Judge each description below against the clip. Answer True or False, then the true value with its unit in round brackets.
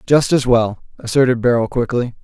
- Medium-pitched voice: False (125 Hz)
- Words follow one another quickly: False (160 wpm)